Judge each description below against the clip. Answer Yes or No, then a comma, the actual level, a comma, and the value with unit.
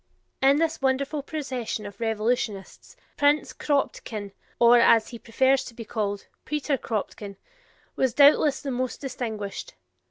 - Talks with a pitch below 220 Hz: No, high, 245 Hz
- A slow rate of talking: Yes, slow, 130 wpm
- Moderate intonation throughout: Yes, average, 4.2 semitones